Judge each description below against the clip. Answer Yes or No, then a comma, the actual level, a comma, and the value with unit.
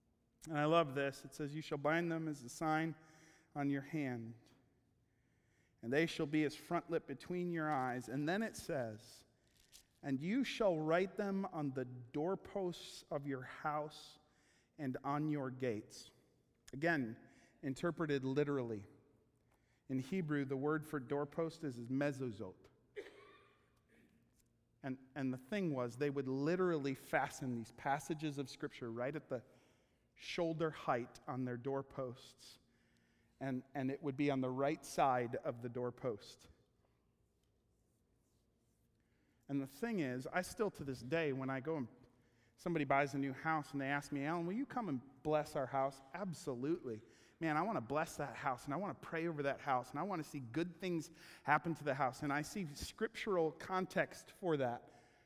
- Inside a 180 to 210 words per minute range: No, average, 165 wpm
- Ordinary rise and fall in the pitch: Yes, average, 4.1 semitones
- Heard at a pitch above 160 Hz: No, medium, 140 Hz